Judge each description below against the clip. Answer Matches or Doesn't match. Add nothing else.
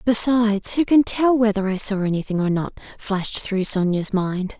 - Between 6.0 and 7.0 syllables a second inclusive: Doesn't match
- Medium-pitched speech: Doesn't match